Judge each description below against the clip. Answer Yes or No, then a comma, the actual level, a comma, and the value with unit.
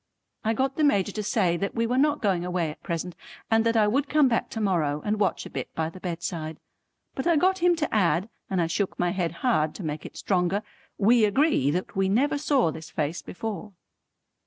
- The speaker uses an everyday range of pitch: No, wide, 6.1 semitones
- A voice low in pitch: No, high, 200 Hz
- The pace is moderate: No, fast, 225 wpm